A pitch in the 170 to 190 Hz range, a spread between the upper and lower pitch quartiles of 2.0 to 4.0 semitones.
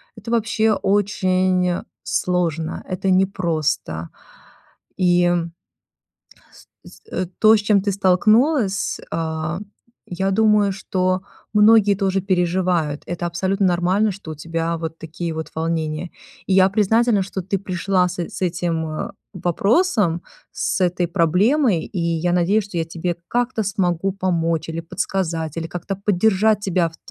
Yes: medium, 185 Hz; average, 3.0 semitones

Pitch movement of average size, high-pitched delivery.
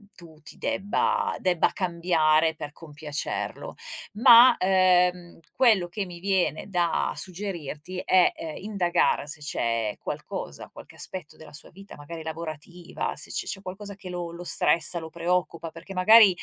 No: average, 3.0 semitones; medium, 175 Hz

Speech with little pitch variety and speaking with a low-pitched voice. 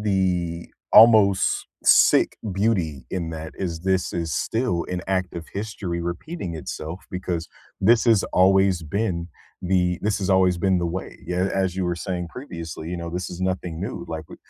Yes: narrow, 2.2 semitones; very low, 90 Hz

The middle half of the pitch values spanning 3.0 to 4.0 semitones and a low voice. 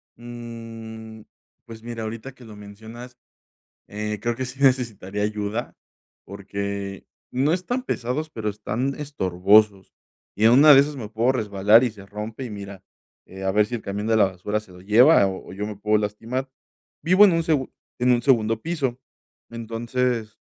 Yes: average, 3.4 semitones; low, 110 Hz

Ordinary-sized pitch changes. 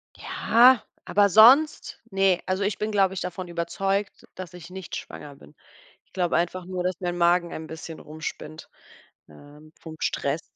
Yes: average, 3.0 semitones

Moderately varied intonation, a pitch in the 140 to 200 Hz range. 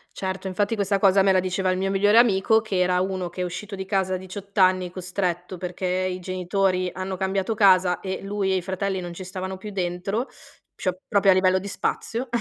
No: narrow, 1.2 semitones; high, 190 Hz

